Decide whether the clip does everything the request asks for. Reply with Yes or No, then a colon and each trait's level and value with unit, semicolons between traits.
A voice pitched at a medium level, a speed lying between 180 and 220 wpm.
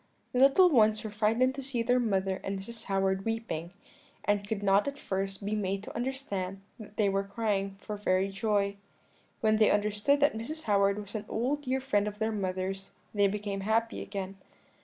No: high, 210 Hz; average, 190 wpm